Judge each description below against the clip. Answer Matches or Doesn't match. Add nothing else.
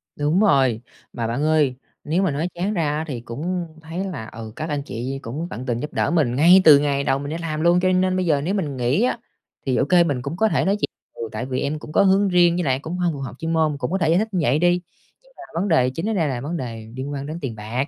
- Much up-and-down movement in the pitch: Doesn't match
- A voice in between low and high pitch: Matches